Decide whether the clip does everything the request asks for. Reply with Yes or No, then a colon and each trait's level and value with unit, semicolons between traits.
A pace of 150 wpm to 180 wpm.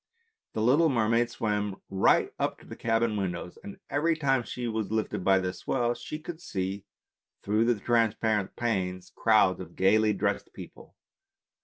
Yes: average, 165 wpm